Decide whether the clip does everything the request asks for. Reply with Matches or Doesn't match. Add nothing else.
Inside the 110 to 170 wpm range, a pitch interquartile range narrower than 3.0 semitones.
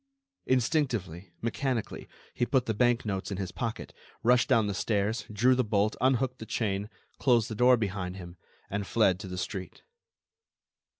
Doesn't match